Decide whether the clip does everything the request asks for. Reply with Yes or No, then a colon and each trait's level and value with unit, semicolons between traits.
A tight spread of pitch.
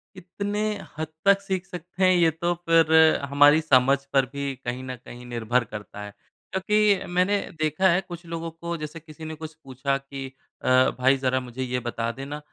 No: average, 5.1 semitones